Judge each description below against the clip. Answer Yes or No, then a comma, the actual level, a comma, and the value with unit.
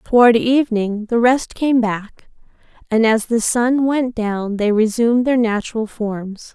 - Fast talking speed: No, average, 155 wpm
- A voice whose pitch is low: No, high, 230 Hz